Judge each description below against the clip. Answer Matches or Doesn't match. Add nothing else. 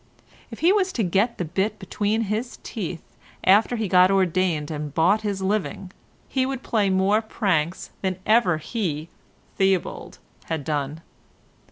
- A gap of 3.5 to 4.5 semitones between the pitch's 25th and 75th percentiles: Matches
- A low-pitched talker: Doesn't match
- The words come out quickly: Doesn't match